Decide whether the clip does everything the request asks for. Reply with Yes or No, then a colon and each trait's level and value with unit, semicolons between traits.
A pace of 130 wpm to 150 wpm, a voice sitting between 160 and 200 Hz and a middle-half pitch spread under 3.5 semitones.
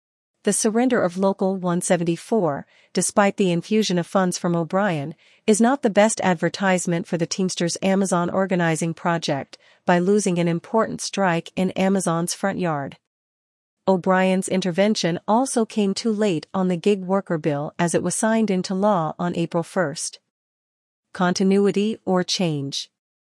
Yes: average, 140 wpm; medium, 185 Hz; average, 2.9 semitones